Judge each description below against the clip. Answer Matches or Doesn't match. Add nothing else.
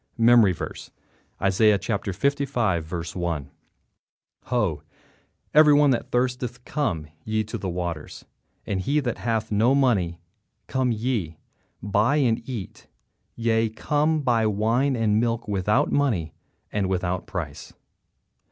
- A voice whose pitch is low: Matches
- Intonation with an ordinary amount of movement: Matches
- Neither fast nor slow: Doesn't match